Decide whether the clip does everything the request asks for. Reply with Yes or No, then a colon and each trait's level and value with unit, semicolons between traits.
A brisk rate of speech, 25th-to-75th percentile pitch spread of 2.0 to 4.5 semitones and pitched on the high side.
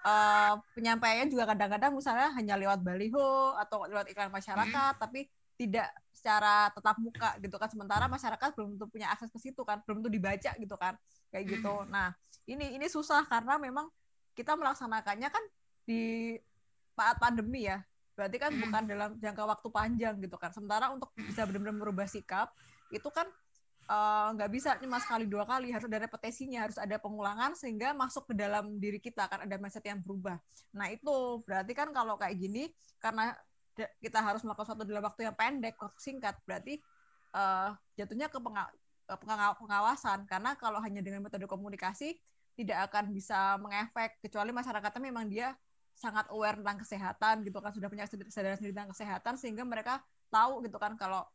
Yes: fast, 170 wpm; average, 3.0 semitones; high, 215 Hz